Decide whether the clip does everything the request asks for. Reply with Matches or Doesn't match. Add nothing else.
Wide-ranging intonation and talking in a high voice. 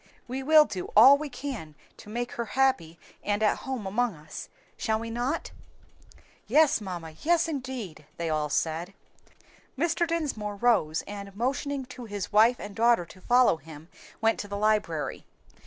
Matches